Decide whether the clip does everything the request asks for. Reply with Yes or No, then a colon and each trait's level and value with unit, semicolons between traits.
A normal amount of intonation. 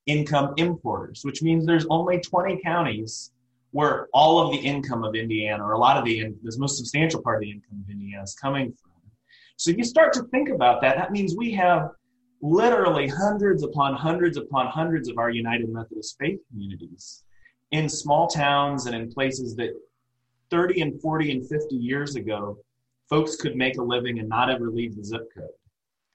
No: wide, 5.9 semitones